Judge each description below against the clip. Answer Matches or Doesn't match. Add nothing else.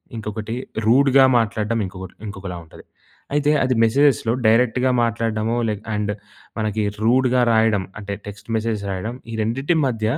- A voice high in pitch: Doesn't match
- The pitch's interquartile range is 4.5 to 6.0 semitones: Doesn't match